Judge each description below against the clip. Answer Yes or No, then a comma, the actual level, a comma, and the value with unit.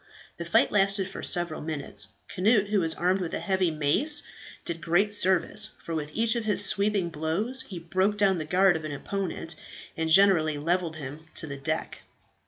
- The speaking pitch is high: No, medium, 180 Hz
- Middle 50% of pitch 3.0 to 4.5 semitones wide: Yes, average, 3.9 semitones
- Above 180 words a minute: Yes, average, 190 wpm